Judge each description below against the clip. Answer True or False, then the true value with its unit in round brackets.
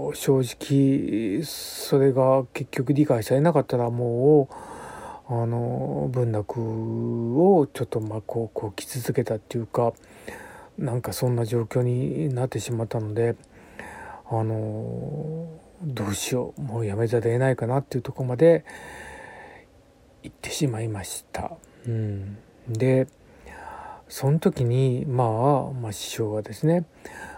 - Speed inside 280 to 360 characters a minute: False (250 characters per minute)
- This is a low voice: True (125 Hz)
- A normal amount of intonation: True (3.7 semitones)